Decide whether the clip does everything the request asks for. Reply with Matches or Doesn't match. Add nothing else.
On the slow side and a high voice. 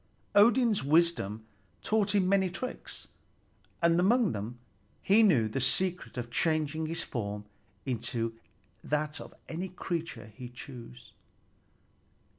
Doesn't match